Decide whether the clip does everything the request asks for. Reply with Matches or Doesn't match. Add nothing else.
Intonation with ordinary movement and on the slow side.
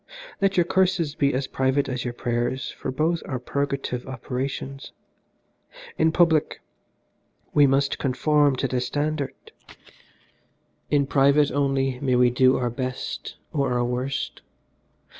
Doesn't match